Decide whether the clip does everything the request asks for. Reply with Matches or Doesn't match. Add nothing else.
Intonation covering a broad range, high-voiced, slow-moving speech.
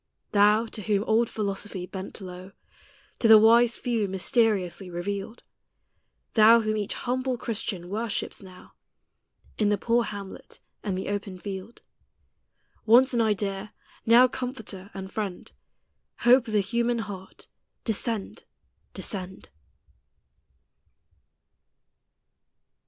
Doesn't match